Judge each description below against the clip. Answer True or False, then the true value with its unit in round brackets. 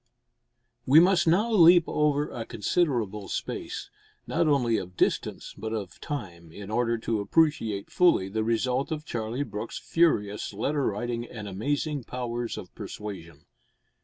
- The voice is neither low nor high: False (120 Hz)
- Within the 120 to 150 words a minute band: True (140 wpm)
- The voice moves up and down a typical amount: False (6.3 semitones)